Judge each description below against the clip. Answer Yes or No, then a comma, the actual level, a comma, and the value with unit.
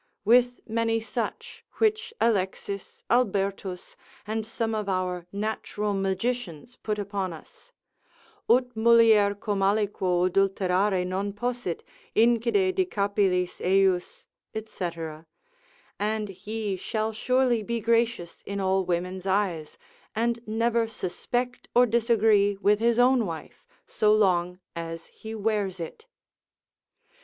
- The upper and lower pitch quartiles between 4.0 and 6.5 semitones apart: No, average, 3.5 semitones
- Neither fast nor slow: No, slow, 115 wpm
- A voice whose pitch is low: No, high, 210 Hz